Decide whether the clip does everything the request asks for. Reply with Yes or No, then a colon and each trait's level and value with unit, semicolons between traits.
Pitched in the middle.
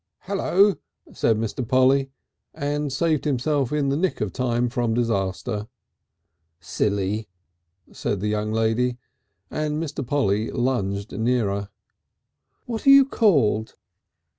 No: low, 125 Hz